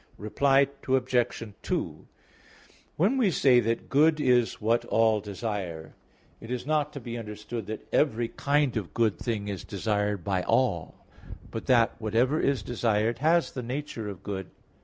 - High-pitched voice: No, low, 115 Hz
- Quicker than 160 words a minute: No, average, 155 wpm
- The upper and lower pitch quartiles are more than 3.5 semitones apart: Yes, average, 4.3 semitones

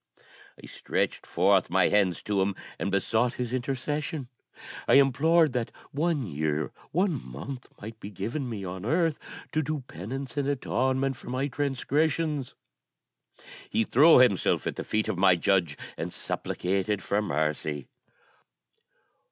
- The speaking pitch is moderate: No, low, 125 Hz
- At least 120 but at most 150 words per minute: Yes, average, 145 wpm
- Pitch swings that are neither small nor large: No, wide, 6.4 semitones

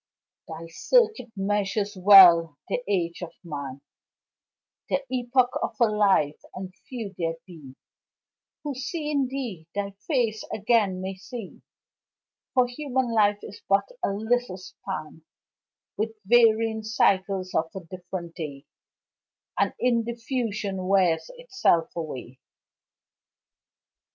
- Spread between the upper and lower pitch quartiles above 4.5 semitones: Yes, average, 5.2 semitones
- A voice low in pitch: No, high, 200 Hz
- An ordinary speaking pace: No, slow, 115 wpm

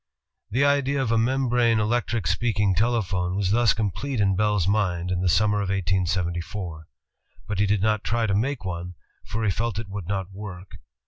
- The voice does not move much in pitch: No, average, 3.7 semitones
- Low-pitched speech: Yes, low, 100 Hz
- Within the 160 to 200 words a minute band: Yes, average, 185 wpm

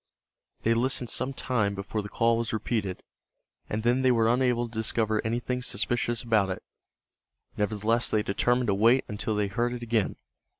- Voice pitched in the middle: No, low, 115 Hz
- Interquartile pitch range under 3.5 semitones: Yes, narrow, 2.4 semitones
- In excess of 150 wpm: Yes, average, 170 wpm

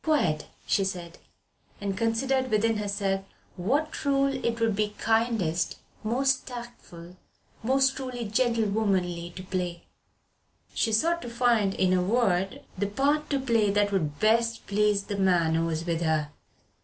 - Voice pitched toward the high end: Yes, high, 210 Hz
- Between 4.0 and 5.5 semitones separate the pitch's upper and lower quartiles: Yes, average, 4.6 semitones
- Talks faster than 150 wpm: No, average, 145 wpm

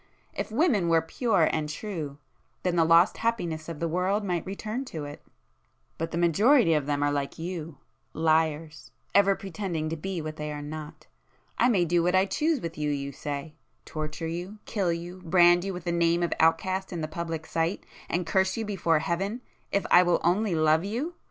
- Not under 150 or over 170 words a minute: No, average, 190 wpm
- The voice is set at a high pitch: No, medium, 170 Hz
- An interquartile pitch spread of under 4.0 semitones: Yes, average, 3.5 semitones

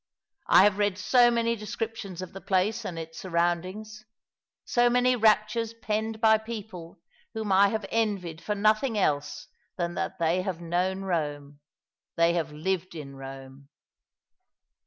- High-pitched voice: Yes, high, 195 Hz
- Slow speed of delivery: No, average, 155 wpm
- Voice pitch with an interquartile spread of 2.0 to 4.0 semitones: No, average, 4.5 semitones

